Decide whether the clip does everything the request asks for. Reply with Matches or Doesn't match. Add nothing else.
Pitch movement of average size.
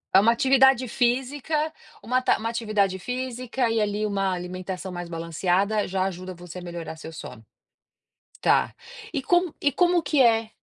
Doesn't match